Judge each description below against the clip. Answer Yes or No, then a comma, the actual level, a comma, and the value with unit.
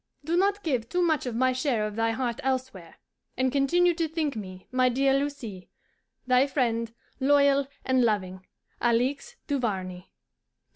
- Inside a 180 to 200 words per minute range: No, average, 150 wpm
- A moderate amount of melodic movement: Yes, average, 4.0 semitones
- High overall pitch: Yes, very high, 255 Hz